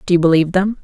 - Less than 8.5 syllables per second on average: No, 8.7 syllables/s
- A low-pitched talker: No, medium, 180 Hz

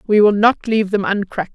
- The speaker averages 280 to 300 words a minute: No, fast, 235 wpm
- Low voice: No, high, 205 Hz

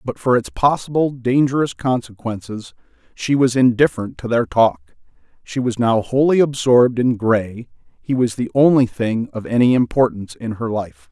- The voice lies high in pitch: No, low, 120 Hz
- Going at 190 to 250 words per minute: No, average, 160 wpm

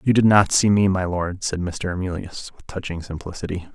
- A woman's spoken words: No, male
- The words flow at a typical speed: No, fast, 210 wpm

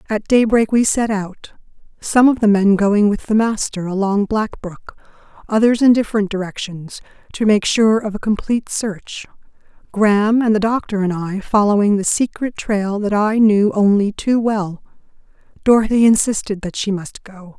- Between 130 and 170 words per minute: Yes, average, 160 wpm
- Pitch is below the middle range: No, high, 210 Hz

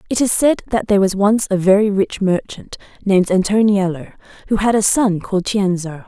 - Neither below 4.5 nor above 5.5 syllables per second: Yes, 5.4 syllables/s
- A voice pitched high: Yes, high, 200 Hz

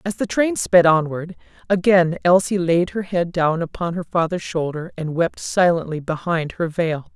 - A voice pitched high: No, medium, 175 Hz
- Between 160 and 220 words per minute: Yes, average, 175 wpm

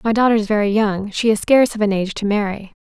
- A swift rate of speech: Yes, fast, 255 wpm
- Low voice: No, high, 210 Hz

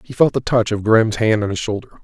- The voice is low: Yes, low, 110 Hz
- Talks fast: Yes, fast, 295 wpm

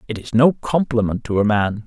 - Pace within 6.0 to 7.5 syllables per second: No, 5.3 syllables/s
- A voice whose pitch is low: Yes, low, 115 Hz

